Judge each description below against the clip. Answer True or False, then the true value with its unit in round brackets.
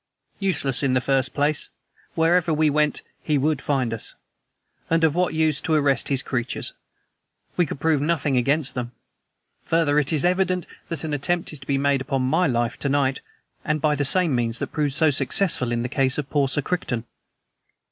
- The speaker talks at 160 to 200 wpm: True (195 wpm)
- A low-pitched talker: False (145 Hz)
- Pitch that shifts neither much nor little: True (3.1 semitones)